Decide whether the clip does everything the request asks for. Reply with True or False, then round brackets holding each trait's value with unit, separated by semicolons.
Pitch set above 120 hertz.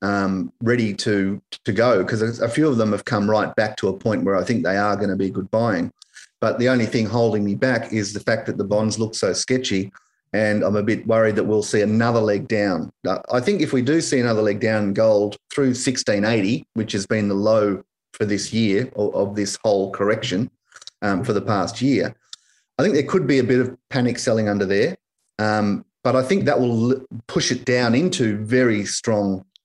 False (110 Hz)